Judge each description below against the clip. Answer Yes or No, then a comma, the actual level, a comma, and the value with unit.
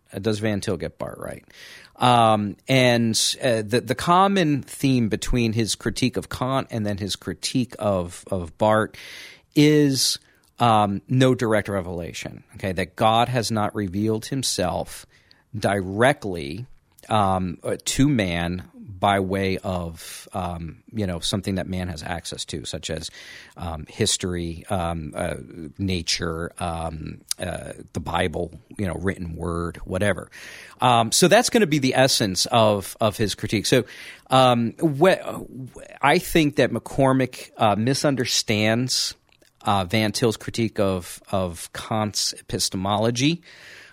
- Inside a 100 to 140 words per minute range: Yes, slow, 135 wpm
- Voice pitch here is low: Yes, low, 105 Hz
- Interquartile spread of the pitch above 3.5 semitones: Yes, average, 5.2 semitones